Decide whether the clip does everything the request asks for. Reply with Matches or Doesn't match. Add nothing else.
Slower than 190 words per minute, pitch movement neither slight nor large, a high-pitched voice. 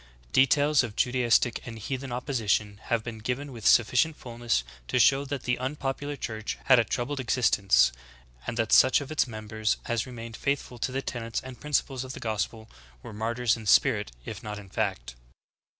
Doesn't match